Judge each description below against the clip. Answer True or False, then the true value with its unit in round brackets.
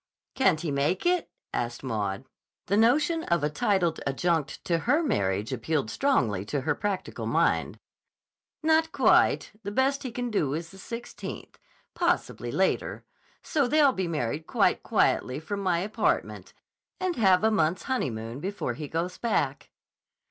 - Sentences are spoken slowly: False (150 wpm)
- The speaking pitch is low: False (180 Hz)